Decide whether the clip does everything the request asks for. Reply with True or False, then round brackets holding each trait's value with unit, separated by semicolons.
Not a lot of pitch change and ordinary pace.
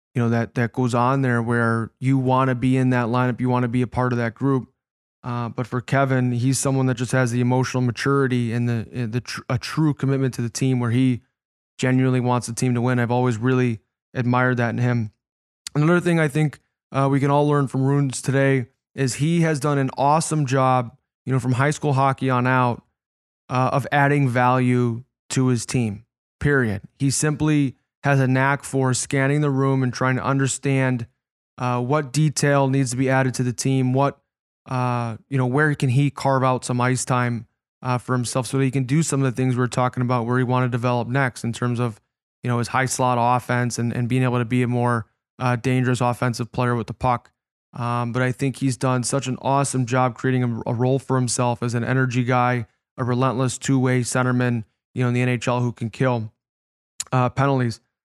False (1.7 semitones; 215 wpm)